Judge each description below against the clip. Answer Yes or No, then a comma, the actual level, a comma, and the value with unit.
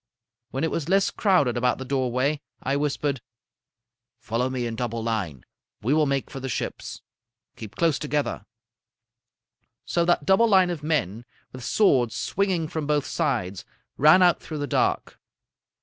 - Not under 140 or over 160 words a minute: Yes, average, 155 wpm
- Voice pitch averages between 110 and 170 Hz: Yes, medium, 140 Hz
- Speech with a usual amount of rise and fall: Yes, average, 4.9 semitones